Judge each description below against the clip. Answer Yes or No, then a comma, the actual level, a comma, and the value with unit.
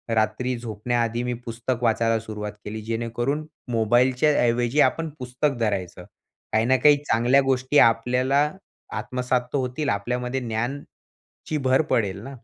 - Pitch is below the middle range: Yes, low, 120 Hz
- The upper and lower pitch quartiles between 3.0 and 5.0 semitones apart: No, narrow, 2.6 semitones